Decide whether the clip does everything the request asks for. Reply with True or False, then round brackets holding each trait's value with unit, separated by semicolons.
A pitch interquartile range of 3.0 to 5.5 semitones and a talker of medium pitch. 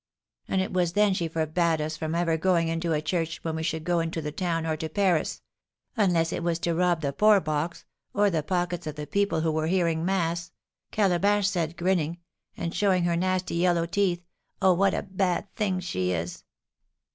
False (2.4 semitones; 170 Hz)